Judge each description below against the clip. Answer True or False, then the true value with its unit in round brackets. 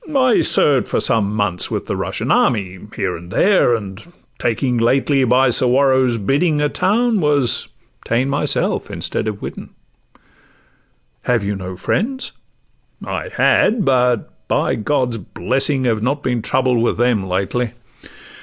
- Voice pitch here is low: True (125 Hz)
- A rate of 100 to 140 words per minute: True (135 wpm)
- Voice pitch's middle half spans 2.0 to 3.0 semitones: False (4.7 semitones)